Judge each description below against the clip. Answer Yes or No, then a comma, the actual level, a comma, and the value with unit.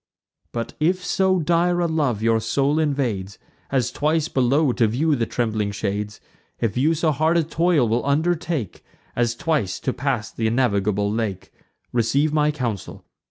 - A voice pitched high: No, low, 130 Hz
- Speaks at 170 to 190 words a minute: No, average, 160 wpm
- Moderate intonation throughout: No, wide, 5.9 semitones